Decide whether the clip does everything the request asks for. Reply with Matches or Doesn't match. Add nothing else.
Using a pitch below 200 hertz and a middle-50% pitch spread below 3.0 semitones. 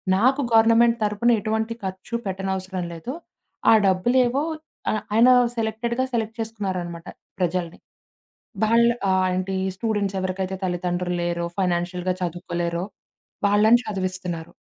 Doesn't match